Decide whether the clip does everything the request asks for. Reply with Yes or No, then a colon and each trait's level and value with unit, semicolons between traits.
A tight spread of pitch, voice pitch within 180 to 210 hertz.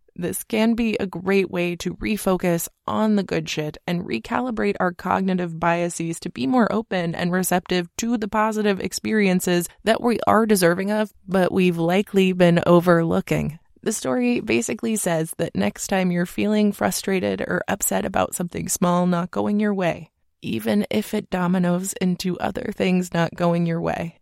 No: average, 3.2 semitones; medium, 185 Hz